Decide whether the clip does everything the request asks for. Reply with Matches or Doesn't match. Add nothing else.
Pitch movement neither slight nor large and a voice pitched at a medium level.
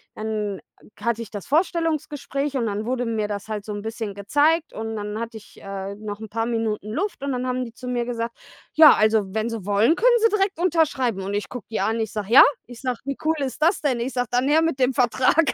Doesn't match